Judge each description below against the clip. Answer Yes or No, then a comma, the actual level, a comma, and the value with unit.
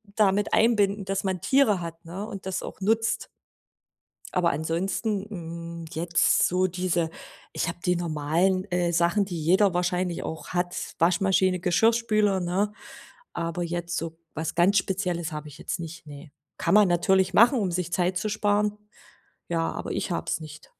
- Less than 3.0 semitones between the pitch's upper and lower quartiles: Yes, narrow, 2.6 semitones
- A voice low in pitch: No, medium, 180 Hz